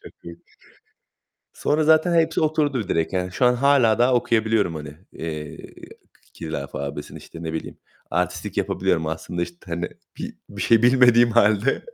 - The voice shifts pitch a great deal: Yes, wide, 7.4 semitones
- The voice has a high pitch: No, low, 110 Hz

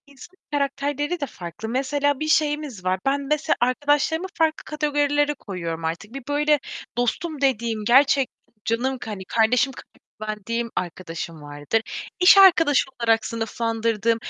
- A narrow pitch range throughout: No, average, 4.9 semitones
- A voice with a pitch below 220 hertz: No, very high, 260 Hz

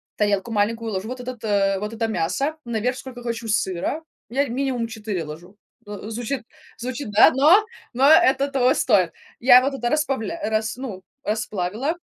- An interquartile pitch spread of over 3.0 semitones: Yes, average, 4.0 semitones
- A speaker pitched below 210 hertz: No, high, 230 Hz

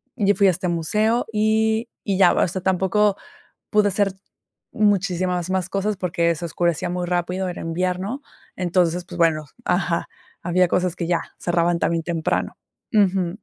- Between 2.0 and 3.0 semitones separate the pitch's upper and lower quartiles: Yes, narrow, 2.4 semitones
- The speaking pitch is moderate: Yes, medium, 180 Hz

